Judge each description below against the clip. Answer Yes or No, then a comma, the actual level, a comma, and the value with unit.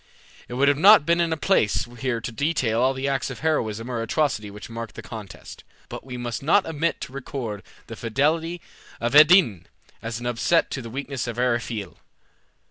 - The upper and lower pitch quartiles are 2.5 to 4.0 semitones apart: No, average, 4.5 semitones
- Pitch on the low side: Yes, low, 125 Hz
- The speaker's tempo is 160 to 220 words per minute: Yes, average, 185 wpm